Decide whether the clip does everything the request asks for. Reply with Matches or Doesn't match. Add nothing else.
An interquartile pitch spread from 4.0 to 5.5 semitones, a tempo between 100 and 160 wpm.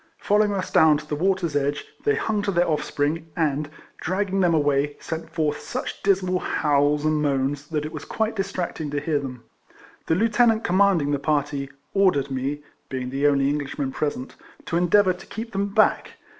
Doesn't match